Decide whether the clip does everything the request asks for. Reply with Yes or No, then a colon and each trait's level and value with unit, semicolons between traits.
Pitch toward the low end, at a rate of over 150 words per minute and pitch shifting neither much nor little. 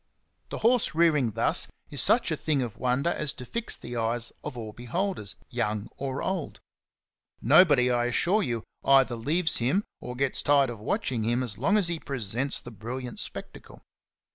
Yes: low, 130 Hz; average, 175 wpm; average, 4.8 semitones